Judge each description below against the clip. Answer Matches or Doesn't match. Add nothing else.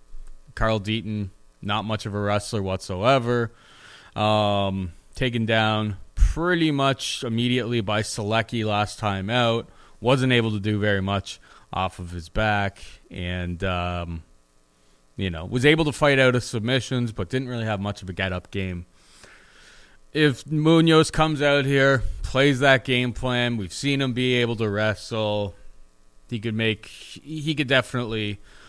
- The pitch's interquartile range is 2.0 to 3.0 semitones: Doesn't match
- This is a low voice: Matches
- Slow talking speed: Doesn't match